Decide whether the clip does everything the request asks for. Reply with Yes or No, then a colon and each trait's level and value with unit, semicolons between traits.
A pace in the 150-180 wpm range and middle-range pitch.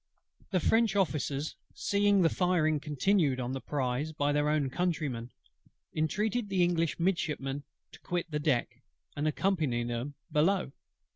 No: average, 140 wpm; medium, 155 Hz